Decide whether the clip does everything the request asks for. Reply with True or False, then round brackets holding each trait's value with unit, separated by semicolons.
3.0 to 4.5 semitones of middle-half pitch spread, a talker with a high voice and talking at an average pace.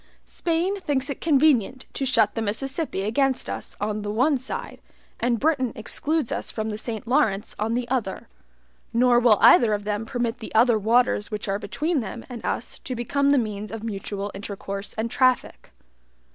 True (3.9 semitones; 235 Hz; 180 wpm)